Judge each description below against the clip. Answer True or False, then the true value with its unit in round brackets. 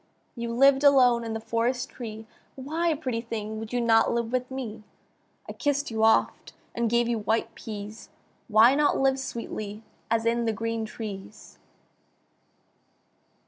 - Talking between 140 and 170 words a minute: True (150 wpm)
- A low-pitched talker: False (230 Hz)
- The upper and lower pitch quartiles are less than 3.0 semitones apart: True (2.5 semitones)